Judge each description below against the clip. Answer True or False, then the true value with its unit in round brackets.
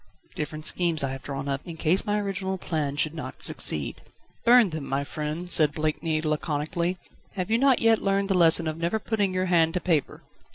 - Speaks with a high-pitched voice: False (165 Hz)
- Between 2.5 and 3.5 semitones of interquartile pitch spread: False (3.9 semitones)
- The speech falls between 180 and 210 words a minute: True (200 wpm)